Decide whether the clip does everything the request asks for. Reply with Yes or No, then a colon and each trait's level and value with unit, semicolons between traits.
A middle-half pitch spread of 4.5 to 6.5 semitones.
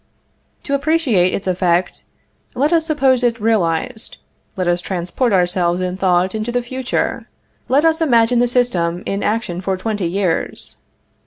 Yes: wide, 5.6 semitones